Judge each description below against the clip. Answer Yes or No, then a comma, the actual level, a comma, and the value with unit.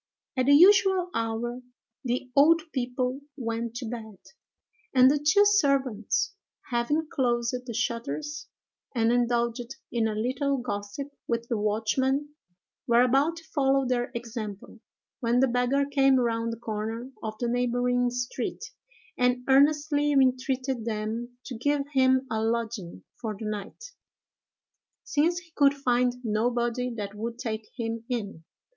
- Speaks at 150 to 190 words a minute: No, average, 140 wpm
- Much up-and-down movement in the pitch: No, average, 3.1 semitones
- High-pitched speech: Yes, high, 245 Hz